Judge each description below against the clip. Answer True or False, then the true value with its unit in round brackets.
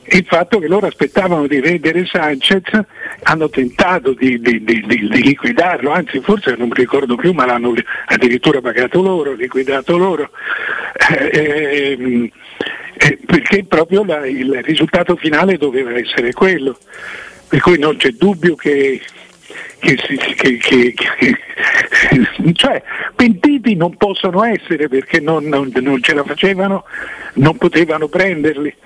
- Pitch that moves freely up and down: True (5.9 semitones)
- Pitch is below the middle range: False (160 Hz)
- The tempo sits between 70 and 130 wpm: False (140 wpm)